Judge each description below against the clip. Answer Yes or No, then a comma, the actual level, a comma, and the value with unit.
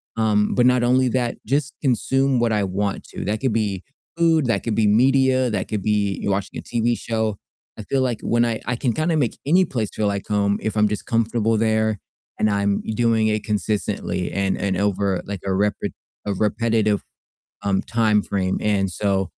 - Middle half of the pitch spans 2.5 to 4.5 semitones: Yes, average, 2.8 semitones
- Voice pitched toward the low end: Yes, low, 110 Hz